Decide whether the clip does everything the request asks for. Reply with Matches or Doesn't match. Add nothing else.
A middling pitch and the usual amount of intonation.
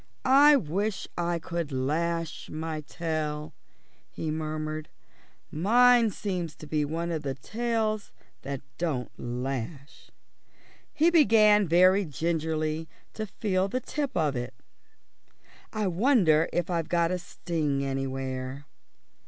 Matches